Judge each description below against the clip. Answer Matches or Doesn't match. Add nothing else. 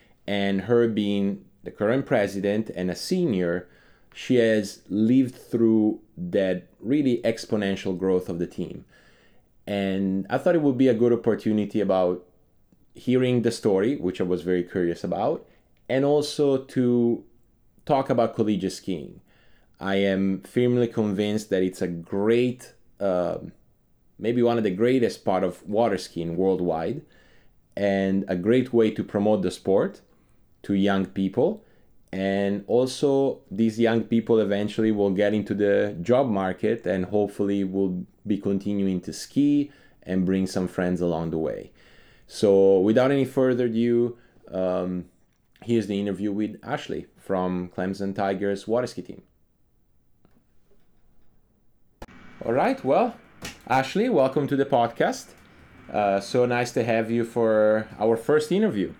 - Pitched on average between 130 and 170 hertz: Doesn't match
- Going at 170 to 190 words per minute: Doesn't match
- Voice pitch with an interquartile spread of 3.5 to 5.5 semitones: Matches